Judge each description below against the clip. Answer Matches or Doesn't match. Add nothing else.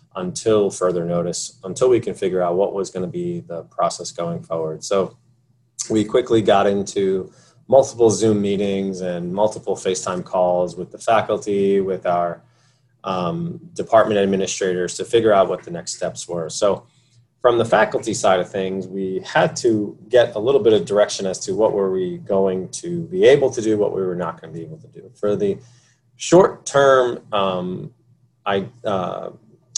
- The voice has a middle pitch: Doesn't match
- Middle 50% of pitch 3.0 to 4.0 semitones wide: Doesn't match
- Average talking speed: Matches